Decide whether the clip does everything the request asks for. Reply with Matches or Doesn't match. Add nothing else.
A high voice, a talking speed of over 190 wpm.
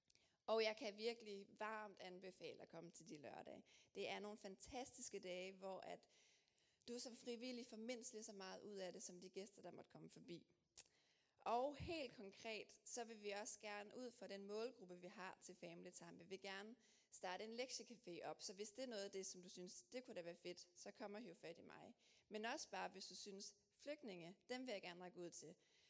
Matches